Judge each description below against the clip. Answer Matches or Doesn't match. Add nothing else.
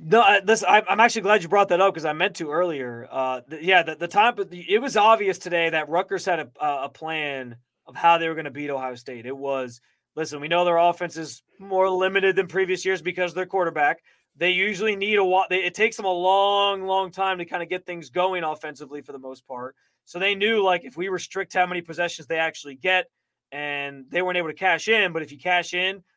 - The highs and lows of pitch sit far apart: Doesn't match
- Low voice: Doesn't match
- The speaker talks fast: Matches